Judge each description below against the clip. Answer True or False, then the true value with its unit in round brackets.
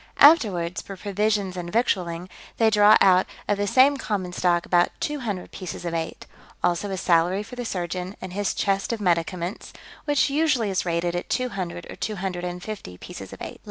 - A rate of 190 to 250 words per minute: True (195 wpm)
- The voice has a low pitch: False (190 Hz)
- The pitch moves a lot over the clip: False (3.3 semitones)